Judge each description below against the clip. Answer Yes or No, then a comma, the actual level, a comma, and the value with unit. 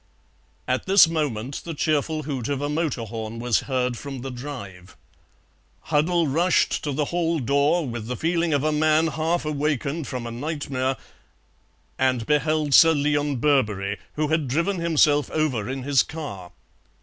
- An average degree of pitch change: Yes, average, 3.7 semitones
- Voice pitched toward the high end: No, medium, 145 Hz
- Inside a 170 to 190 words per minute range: No, average, 160 wpm